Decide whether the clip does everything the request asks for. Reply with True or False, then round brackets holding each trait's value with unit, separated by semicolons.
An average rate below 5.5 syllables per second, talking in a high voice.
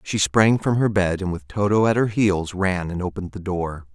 False (5.0 syllables/s; 95 Hz)